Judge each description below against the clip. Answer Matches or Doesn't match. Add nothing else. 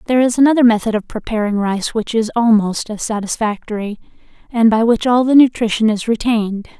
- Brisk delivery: Doesn't match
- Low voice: Doesn't match